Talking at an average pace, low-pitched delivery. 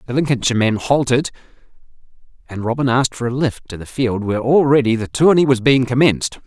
Yes: average, 185 wpm; low, 125 Hz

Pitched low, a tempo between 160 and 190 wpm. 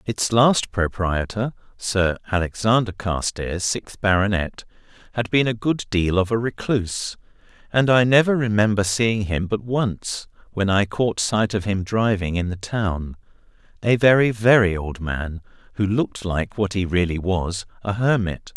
No: low, 105 Hz; average, 150 wpm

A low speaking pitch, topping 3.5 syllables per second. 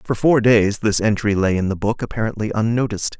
Yes: low, 110 Hz; 5.8 syllables/s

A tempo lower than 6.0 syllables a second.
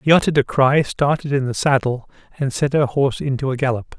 No: 6.1 syllables/s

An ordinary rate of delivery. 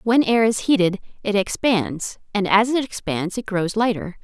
Yes: average, 185 wpm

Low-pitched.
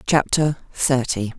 Yes: low, 130 Hz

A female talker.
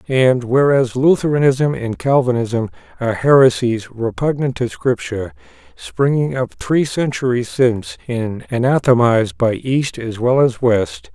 No: male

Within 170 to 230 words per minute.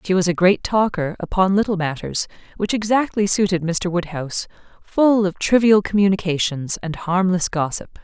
No: average, 150 wpm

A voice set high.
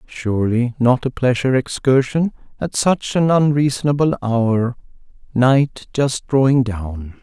No: low, 130 Hz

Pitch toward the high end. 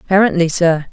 No: medium, 175 Hz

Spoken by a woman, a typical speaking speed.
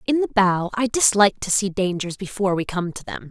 No: female; fast, 235 wpm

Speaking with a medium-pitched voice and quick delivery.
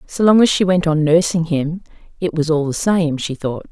Yes: medium, 165 Hz; fast, 240 wpm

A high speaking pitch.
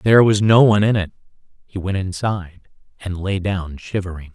No: very low, 95 Hz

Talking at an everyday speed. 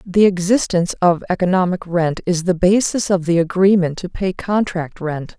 Yes: average, 165 wpm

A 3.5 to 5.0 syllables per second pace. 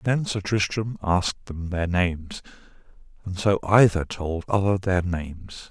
Yes: 4.6 syllables/s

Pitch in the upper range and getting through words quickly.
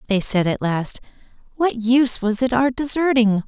No: high, 235 Hz; average, 175 wpm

